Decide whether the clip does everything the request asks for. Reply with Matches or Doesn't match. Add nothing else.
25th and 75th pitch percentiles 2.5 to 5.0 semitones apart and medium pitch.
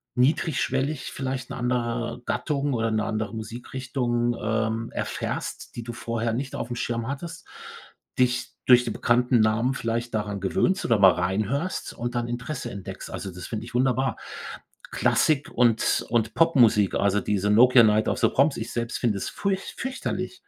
Doesn't match